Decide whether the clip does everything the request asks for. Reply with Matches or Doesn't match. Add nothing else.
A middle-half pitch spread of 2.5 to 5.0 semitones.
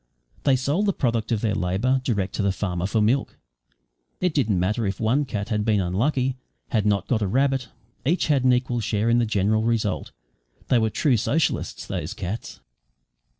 Matches